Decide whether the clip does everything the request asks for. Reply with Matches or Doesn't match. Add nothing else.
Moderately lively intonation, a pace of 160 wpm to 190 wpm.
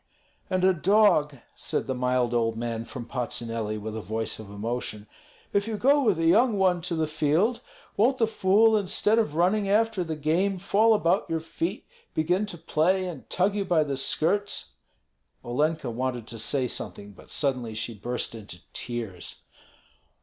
Doesn't match